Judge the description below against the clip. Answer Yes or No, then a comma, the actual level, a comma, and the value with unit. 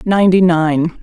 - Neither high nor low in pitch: Yes, medium, 170 Hz